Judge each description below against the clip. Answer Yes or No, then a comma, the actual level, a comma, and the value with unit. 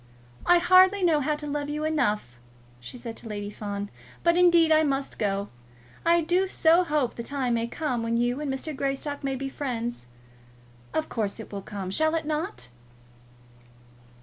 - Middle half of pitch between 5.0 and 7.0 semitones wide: Yes, wide, 5.6 semitones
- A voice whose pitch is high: Yes, very high, 275 Hz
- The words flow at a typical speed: Yes, average, 175 wpm